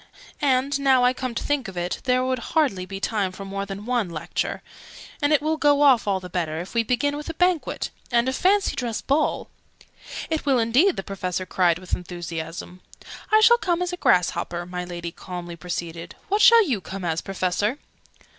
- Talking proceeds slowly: No, fast, 205 wpm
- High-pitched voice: Yes, high, 225 Hz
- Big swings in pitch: Yes, wide, 8.1 semitones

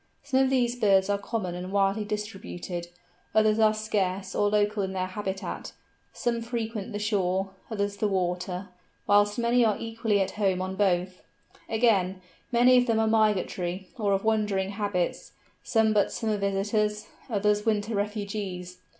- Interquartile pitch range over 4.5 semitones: No, narrow, 2.4 semitones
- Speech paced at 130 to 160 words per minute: Yes, average, 155 wpm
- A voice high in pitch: Yes, high, 205 Hz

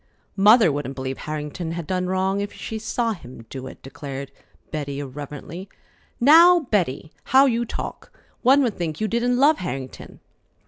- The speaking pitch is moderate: Yes, medium, 180 Hz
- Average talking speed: Yes, average, 155 wpm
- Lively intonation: Yes, wide, 8.6 semitones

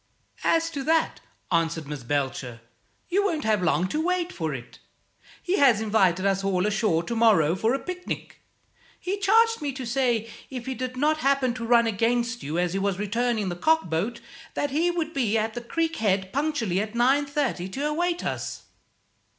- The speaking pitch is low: No, high, 235 Hz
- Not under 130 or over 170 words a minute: No, average, 185 wpm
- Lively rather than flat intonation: Yes, wide, 7.6 semitones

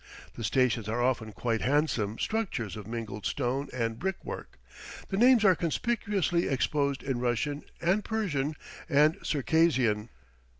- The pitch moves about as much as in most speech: No, wide, 6.5 semitones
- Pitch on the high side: No, low, 135 Hz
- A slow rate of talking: Yes, slow, 130 wpm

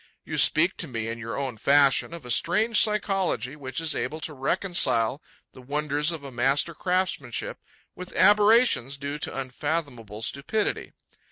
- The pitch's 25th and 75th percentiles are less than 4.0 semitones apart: No, wide, 5.5 semitones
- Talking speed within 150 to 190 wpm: Yes, average, 155 wpm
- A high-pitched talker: No, medium, 145 Hz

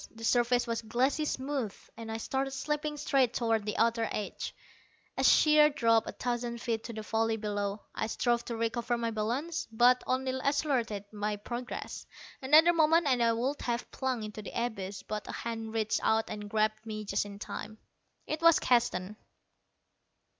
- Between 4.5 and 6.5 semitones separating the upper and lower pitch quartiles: No, average, 3.2 semitones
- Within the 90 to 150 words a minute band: No, average, 175 wpm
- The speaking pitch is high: Yes, high, 235 Hz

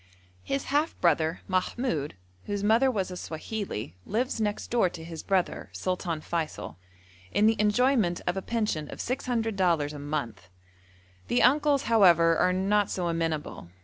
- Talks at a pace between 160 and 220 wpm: No, average, 150 wpm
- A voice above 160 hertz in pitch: Yes, medium, 185 Hz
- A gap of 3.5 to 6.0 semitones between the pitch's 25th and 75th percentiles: Yes, wide, 5.5 semitones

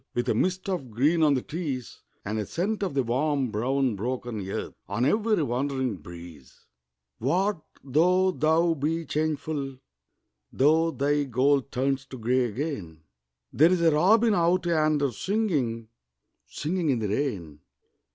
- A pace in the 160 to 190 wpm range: No, average, 140 wpm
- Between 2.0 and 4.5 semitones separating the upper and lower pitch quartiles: No, average, 5.3 semitones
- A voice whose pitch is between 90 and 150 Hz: Yes, medium, 140 Hz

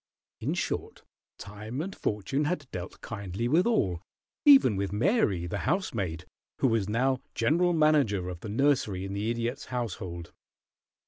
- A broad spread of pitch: Yes, wide, 6.9 semitones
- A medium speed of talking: Yes, average, 145 wpm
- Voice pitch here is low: Yes, low, 115 Hz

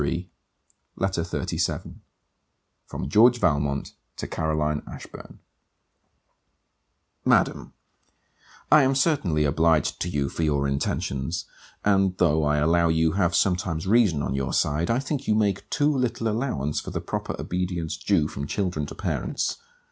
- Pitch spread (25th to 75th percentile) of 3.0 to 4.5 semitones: No, wide, 5.5 semitones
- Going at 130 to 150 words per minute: Yes, average, 140 wpm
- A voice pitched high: No, very low, 85 Hz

